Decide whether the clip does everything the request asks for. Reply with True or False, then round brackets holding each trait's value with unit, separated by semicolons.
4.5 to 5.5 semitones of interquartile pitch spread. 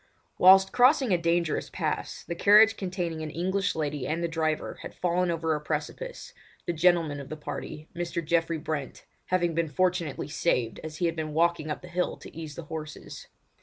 False (2.6 semitones)